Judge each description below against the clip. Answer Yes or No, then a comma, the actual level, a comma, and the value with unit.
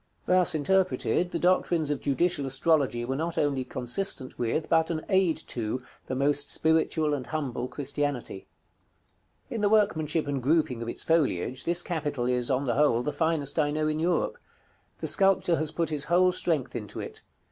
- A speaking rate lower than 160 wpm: No, average, 175 wpm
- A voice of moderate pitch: Yes, medium, 150 Hz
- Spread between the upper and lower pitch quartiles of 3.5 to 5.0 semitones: Yes, average, 4.2 semitones